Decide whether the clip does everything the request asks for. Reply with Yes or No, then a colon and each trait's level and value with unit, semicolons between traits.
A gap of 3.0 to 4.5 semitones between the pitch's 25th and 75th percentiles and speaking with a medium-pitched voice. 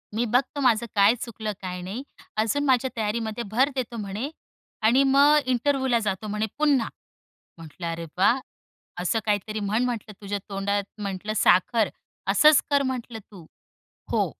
No: average, 4.0 semitones; high, 220 Hz